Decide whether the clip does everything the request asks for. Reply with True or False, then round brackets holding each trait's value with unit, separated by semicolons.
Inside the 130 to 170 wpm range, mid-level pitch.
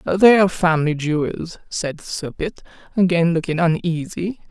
True (135 wpm; 170 Hz)